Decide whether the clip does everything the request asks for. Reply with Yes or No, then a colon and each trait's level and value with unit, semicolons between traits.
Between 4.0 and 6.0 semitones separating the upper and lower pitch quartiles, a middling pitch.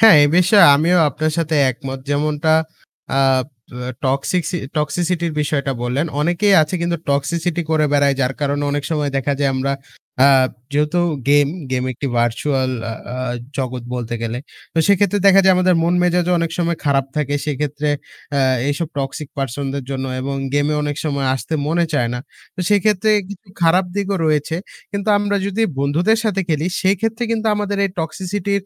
Yes: average, 4.4 semitones; medium, 155 Hz